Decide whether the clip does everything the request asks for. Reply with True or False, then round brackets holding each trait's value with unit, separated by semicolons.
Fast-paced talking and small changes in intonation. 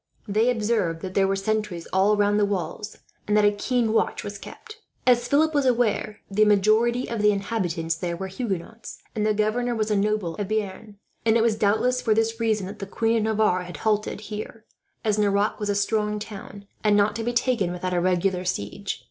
True (210 wpm; 2.3 semitones)